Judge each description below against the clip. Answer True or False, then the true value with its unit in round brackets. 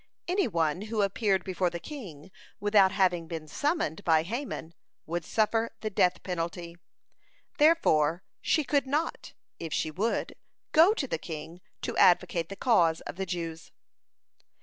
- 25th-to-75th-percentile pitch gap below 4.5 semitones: False (5.5 semitones)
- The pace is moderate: True (150 wpm)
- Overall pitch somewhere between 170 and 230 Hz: True (185 Hz)